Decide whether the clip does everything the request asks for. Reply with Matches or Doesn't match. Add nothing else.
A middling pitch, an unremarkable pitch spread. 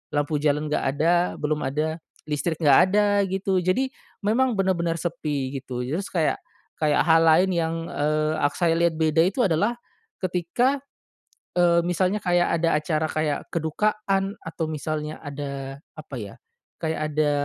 Matches